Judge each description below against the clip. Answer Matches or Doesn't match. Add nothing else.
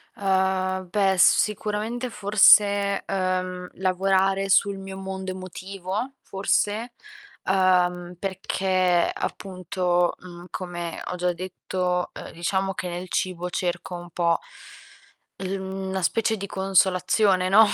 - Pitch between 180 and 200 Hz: Matches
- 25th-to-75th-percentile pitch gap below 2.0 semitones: Matches